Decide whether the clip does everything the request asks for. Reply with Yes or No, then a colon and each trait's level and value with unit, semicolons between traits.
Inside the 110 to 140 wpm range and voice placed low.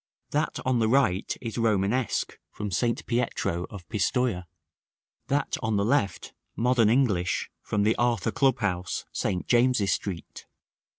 Yes: slow, 135 wpm; low, 110 Hz